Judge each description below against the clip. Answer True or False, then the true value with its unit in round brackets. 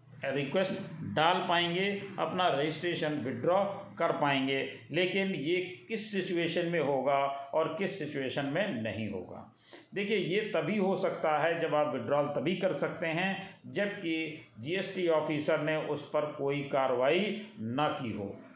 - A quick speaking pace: False (140 wpm)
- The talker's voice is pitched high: False (165 Hz)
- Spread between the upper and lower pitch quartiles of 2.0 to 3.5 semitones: False (4.7 semitones)